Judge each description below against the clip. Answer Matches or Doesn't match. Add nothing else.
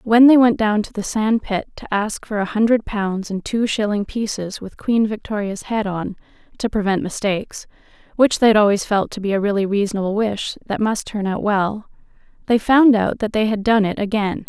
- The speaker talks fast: Matches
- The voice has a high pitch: Matches